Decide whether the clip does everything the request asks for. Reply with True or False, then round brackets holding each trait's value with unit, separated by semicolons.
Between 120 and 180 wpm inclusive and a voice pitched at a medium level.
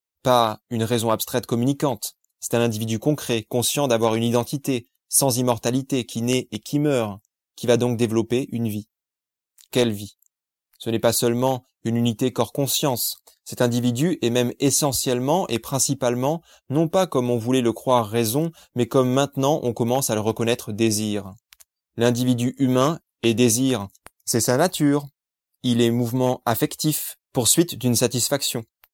False (150 wpm; 125 Hz)